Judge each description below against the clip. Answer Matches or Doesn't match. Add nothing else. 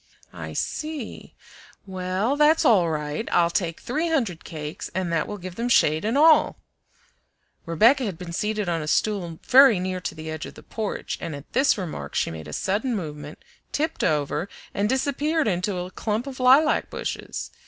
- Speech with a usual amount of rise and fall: Doesn't match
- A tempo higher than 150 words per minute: Matches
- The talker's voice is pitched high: Matches